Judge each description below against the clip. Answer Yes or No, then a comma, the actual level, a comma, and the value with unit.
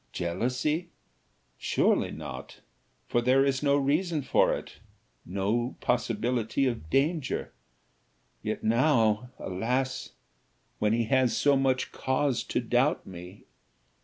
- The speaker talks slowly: Yes, slow, 110 wpm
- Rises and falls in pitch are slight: No, average, 3.4 semitones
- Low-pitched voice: Yes, low, 125 Hz